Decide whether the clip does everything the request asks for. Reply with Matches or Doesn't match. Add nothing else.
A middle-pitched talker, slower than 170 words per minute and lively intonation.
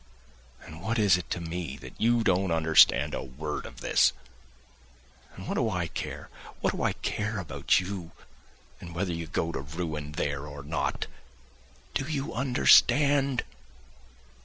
Doesn't match